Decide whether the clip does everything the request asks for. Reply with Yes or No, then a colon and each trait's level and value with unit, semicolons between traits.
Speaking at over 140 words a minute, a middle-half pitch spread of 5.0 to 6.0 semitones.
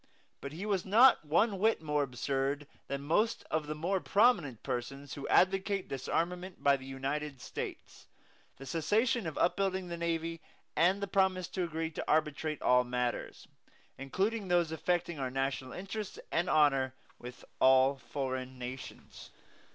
Yes: average, 150 wpm; wide, 5.5 semitones